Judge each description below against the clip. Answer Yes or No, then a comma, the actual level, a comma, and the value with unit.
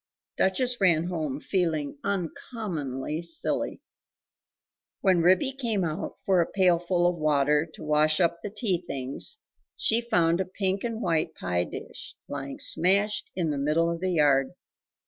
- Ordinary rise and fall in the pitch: Yes, average, 3.8 semitones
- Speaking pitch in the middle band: Yes, medium, 170 Hz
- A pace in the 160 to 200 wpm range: No, average, 145 wpm